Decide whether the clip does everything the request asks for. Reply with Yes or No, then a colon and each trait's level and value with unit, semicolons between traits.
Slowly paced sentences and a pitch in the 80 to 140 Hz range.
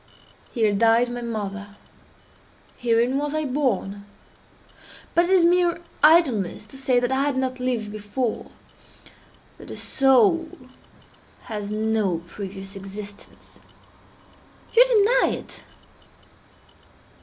No: slow, 105 wpm; high, 240 Hz